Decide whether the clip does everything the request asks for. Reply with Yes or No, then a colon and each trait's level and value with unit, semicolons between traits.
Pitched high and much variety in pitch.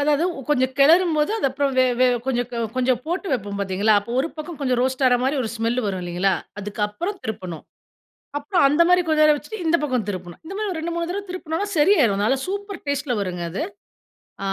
Yes: very high, 275 Hz; wide, 7.1 semitones